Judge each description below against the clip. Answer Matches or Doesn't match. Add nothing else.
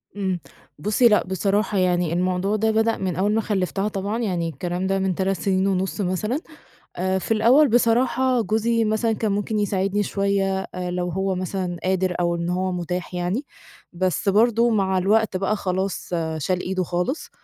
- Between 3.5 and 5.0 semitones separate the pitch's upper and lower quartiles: Doesn't match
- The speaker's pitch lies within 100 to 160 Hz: Doesn't match